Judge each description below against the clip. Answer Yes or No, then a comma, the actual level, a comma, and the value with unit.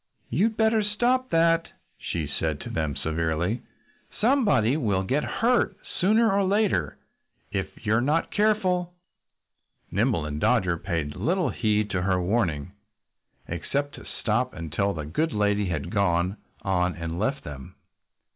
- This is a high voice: No, low, 105 Hz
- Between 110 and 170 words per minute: Yes, slow, 135 wpm